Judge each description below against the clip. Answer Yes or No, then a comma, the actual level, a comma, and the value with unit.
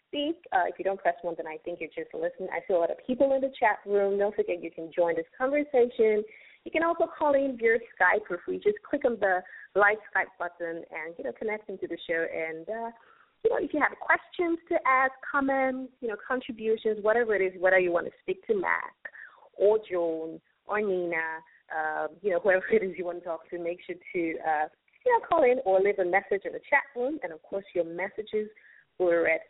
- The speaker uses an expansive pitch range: Yes, wide, 7.7 semitones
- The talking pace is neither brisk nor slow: No, fast, 235 wpm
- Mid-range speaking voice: No, high, 205 Hz